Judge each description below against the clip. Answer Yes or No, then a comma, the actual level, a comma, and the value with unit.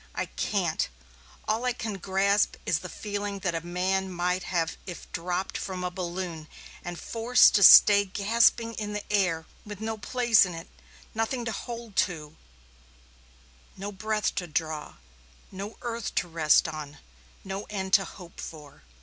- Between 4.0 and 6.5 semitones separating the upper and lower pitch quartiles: No, average, 3.4 semitones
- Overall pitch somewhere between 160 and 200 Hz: Yes, high, 190 Hz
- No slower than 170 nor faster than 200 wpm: No, average, 160 wpm